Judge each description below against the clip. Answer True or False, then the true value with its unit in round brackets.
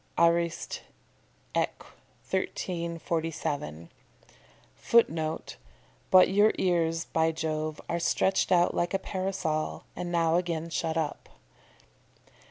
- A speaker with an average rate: False (95 wpm)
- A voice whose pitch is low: False (170 Hz)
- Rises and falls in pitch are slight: True (1.7 semitones)